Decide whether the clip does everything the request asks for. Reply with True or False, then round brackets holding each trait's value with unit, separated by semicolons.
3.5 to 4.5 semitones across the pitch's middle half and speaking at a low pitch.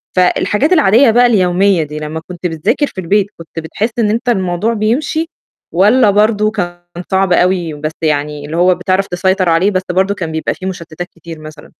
False (4.0 semitones; 185 Hz)